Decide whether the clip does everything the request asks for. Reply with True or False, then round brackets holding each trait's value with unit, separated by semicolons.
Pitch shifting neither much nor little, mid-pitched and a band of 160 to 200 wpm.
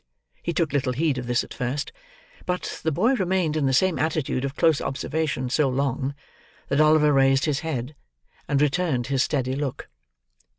True (3.1 semitones; 145 Hz; 175 wpm)